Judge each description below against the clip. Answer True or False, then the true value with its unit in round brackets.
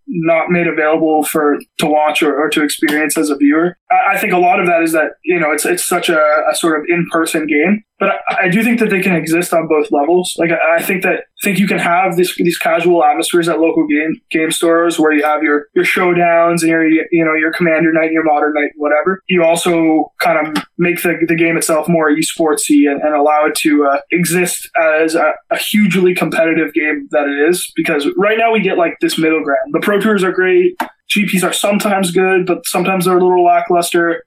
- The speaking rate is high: True (230 wpm)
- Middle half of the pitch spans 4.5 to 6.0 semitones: False (2.8 semitones)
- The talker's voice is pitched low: False (170 Hz)